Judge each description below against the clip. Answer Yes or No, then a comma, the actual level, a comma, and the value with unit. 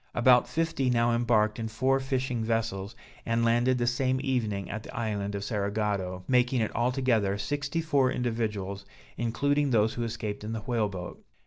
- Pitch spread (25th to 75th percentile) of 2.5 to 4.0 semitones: Yes, average, 3.2 semitones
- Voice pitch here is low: Yes, low, 115 Hz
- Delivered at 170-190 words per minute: No, average, 160 wpm